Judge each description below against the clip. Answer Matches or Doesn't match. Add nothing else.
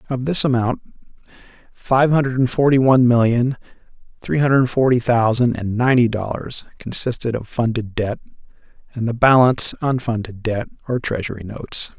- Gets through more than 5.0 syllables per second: Matches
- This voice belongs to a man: Matches